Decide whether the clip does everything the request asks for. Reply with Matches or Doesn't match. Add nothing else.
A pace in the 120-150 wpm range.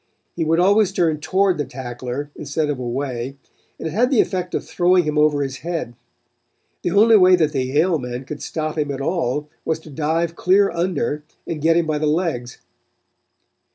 Doesn't match